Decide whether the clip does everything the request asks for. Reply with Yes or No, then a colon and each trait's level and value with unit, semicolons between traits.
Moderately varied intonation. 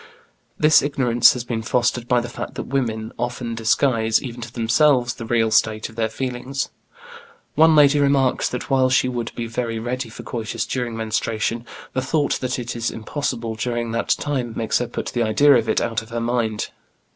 No: narrow, 2.1 semitones